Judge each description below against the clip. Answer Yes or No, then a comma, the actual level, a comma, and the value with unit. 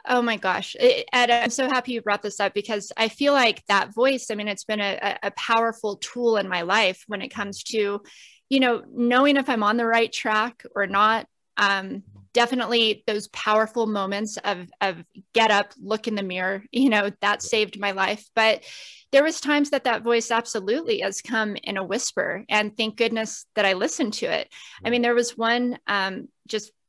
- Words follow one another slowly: No, average, 200 wpm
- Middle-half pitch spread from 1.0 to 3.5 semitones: Yes, average, 2.9 semitones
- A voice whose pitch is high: Yes, high, 220 Hz